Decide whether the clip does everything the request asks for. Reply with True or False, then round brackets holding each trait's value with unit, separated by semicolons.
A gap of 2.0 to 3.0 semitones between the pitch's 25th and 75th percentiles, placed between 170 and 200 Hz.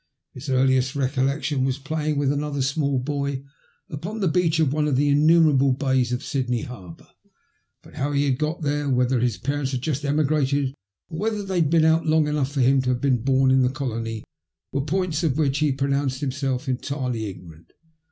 False (2.5 semitones; 140 Hz)